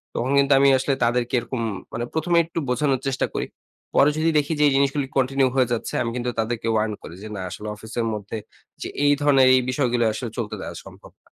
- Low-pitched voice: Yes, low, 130 Hz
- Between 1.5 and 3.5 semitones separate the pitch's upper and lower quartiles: Yes, average, 2.9 semitones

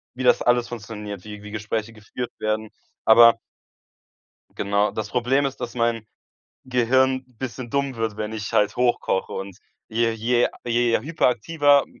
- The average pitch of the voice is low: Yes, low, 115 Hz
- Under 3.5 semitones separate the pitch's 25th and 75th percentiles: Yes, average, 2.7 semitones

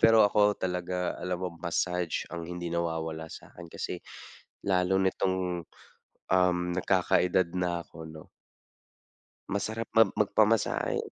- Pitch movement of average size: No, narrow, 1.9 semitones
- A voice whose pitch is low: Yes, very low, 90 Hz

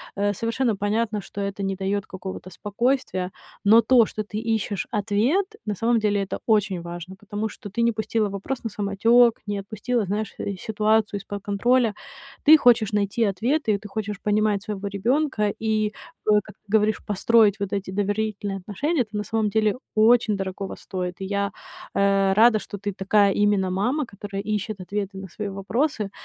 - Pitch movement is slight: Yes, narrow, 1.9 semitones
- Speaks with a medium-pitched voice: No, high, 210 Hz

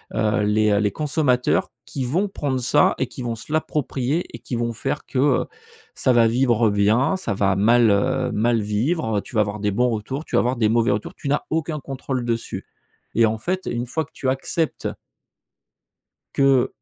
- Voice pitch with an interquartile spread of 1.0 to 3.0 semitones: No, average, 4.2 semitones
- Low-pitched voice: Yes, low, 120 Hz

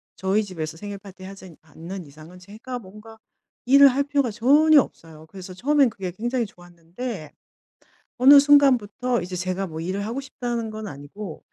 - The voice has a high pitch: Yes, high, 205 Hz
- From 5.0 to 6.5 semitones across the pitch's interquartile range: Yes, wide, 5.6 semitones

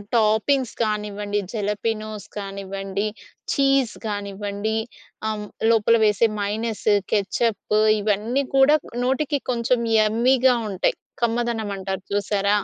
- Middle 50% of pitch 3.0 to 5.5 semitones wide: No, narrow, 2.6 semitones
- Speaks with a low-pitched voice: No, high, 215 Hz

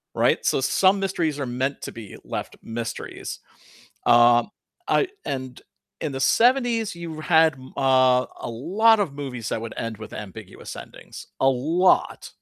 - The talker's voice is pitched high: No, low, 135 Hz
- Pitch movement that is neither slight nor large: No, wide, 6.2 semitones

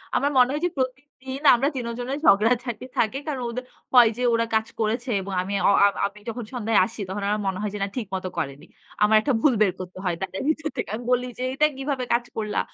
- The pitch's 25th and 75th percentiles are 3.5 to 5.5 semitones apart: Yes, average, 3.8 semitones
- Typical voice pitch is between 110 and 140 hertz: No, high, 235 Hz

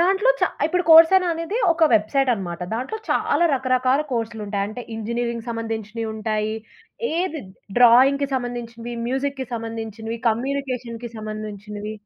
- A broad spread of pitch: No, average, 3.8 semitones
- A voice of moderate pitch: No, high, 235 Hz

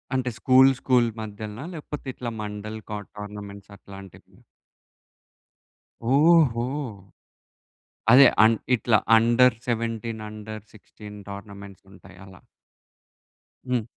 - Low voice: Yes, low, 110 Hz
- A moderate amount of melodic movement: Yes, average, 3.2 semitones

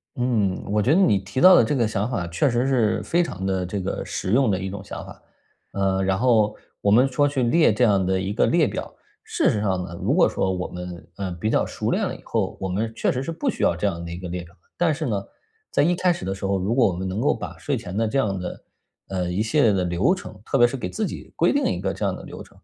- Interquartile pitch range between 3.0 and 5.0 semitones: No, wide, 5.4 semitones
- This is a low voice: Yes, low, 105 Hz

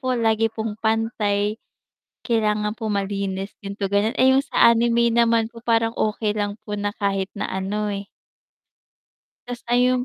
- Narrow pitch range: Yes, narrow, 2.3 semitones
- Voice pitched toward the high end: Yes, high, 220 Hz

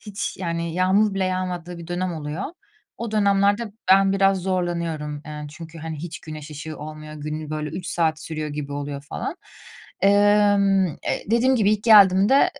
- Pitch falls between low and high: Yes, medium, 175 Hz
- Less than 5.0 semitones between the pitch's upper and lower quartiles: Yes, average, 4.3 semitones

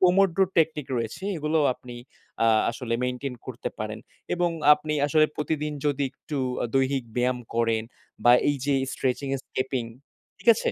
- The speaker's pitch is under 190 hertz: Yes, medium, 140 Hz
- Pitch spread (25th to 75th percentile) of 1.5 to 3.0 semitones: No, average, 3.5 semitones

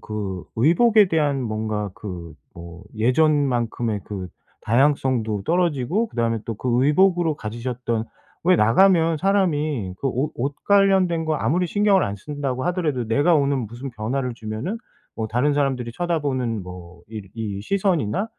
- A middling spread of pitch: No, wide, 6.8 semitones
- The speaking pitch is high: No, low, 130 Hz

